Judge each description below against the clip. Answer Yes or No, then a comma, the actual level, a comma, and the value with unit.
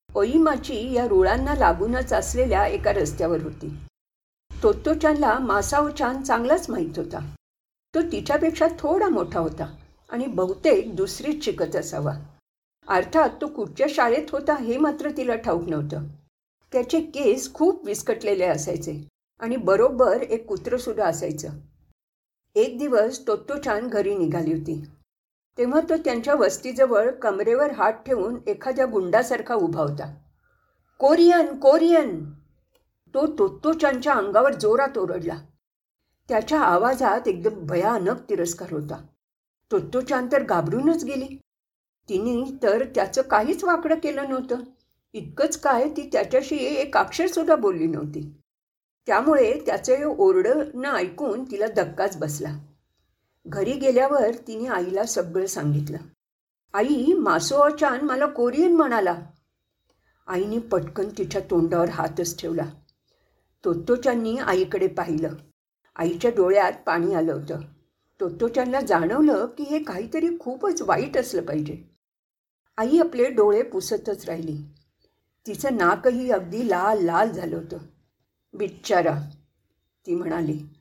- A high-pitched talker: Yes, high, 245 Hz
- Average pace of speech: No, slow, 115 wpm